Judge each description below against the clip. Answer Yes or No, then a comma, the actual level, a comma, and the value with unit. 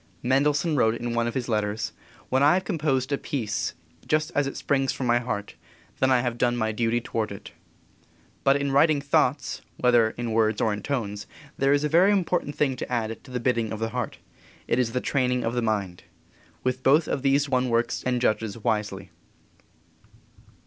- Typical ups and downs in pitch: Yes, average, 3.7 semitones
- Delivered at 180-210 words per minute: Yes, average, 195 wpm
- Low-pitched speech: Yes, low, 125 Hz